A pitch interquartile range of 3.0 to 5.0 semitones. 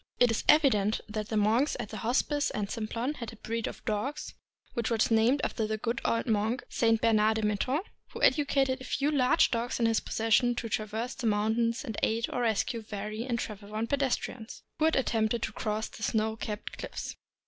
No: narrow, 2.4 semitones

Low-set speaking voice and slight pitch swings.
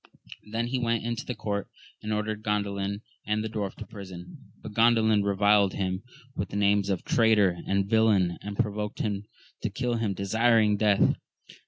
Yes: low, 105 Hz; narrow, 1.9 semitones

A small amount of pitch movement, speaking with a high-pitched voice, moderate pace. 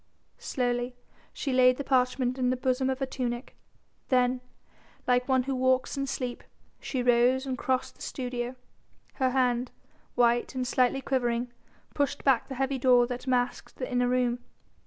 Yes: narrow, 1.1 semitones; very high, 255 Hz; average, 160 wpm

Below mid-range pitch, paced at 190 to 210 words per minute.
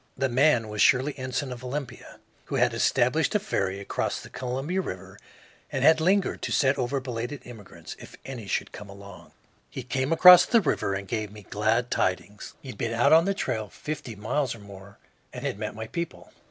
Yes: low, 125 Hz; average, 200 wpm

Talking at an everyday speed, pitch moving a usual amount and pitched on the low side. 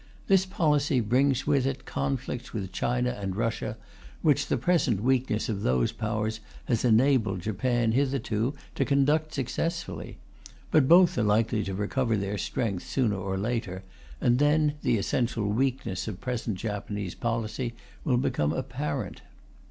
Yes: average, 145 wpm; average, 4.5 semitones; low, 120 Hz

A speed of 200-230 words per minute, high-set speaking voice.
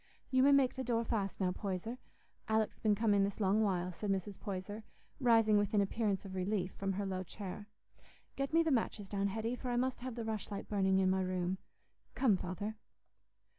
Yes: fast, 205 wpm; high, 205 Hz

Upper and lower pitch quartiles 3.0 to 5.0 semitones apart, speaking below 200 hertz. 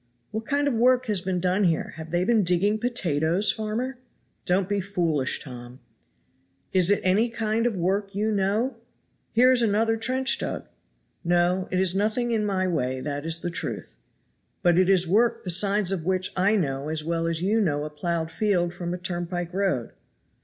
Yes: average, 3.9 semitones; medium, 185 Hz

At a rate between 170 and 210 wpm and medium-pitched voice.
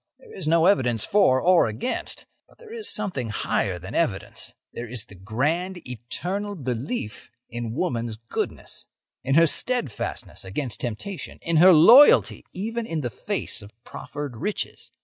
No: average, 150 wpm; medium, 145 Hz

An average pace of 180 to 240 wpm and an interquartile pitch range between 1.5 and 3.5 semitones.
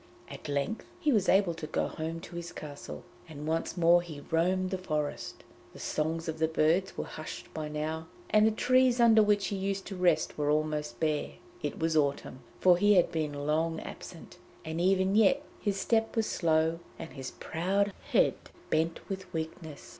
No: average, 185 wpm; average, 3.9 semitones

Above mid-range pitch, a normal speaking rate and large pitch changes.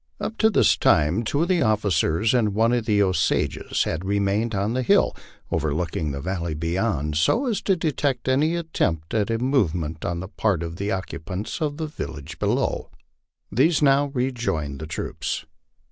No: low, 105 Hz; average, 180 wpm; wide, 7.9 semitones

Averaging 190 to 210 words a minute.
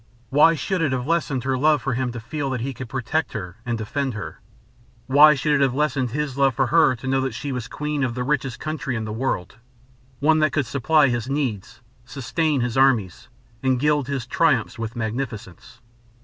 Yes: fast, 205 wpm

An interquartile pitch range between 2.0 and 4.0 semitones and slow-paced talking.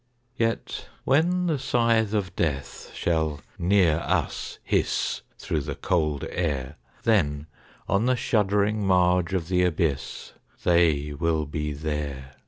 No: wide, 5.4 semitones; slow, 125 wpm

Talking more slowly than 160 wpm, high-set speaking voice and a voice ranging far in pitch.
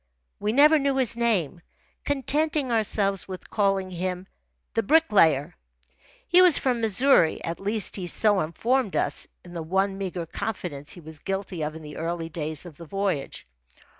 No: average, 165 wpm; high, 195 Hz; wide, 5.7 semitones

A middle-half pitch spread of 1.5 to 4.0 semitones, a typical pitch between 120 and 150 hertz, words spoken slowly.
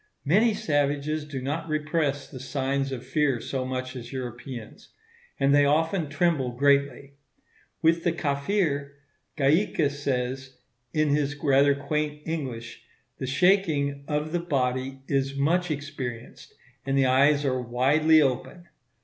Yes: narrow, 2.5 semitones; medium, 140 Hz; slow, 130 wpm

